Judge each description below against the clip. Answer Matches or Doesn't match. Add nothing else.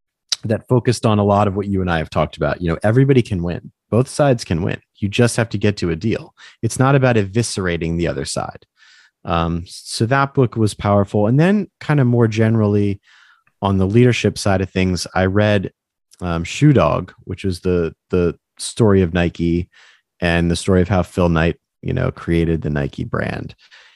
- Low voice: Matches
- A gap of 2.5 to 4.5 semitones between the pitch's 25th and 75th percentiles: Doesn't match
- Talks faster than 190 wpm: Matches